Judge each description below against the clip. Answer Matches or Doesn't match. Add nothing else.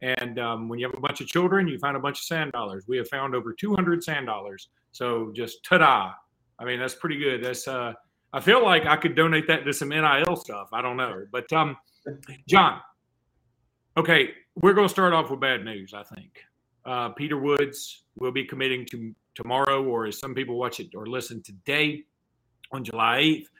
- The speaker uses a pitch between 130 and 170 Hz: Matches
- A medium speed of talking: Doesn't match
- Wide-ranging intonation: Doesn't match